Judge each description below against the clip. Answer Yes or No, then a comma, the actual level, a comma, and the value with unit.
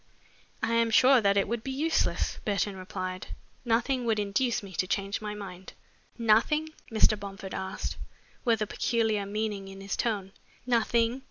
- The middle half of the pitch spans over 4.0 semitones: No, average, 2.9 semitones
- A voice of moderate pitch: No, high, 215 Hz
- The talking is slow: No, average, 160 wpm